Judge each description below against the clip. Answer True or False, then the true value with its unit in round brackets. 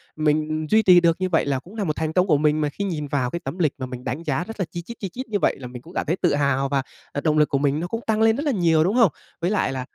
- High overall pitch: False (160 Hz)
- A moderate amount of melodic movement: True (4.6 semitones)